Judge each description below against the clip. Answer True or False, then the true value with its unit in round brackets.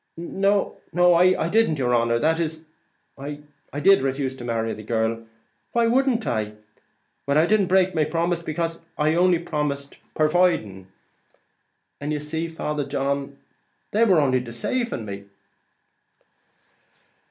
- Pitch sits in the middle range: True (150 Hz)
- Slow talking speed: True (130 wpm)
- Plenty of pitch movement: False (4.9 semitones)